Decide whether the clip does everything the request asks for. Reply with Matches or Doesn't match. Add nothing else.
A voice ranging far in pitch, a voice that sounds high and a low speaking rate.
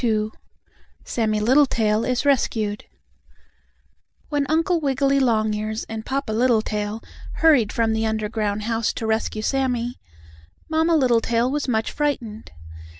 Doesn't match